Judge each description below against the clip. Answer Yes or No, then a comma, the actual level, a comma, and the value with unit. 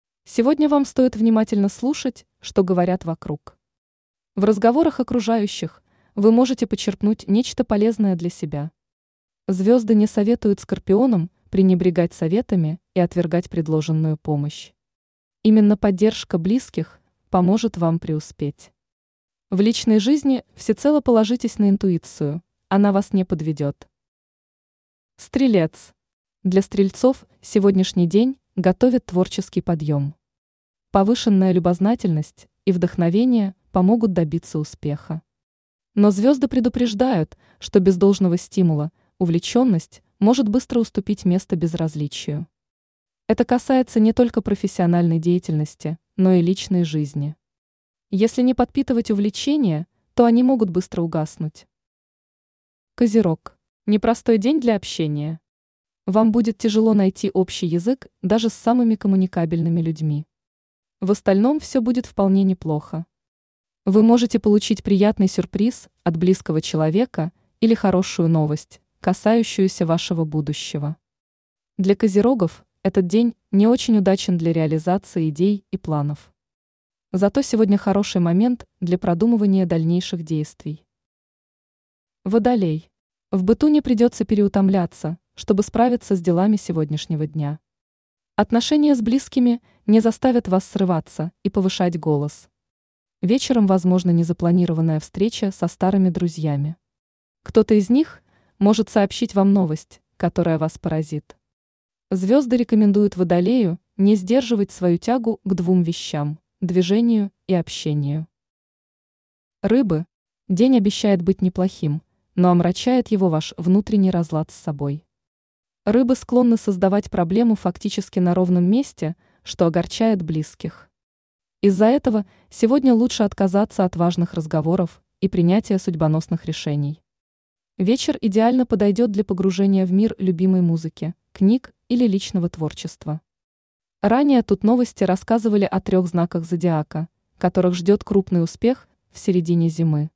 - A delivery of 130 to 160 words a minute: No, average, 115 wpm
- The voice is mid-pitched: No, high, 195 Hz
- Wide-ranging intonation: No, average, 4.7 semitones